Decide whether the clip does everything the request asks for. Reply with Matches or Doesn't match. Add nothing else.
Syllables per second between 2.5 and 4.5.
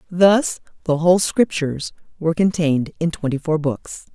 Doesn't match